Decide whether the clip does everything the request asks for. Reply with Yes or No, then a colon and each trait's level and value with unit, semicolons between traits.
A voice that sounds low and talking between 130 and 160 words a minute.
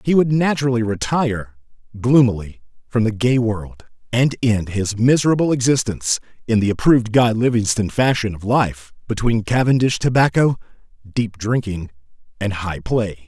Yes: low, 115 Hz; slow, 135 wpm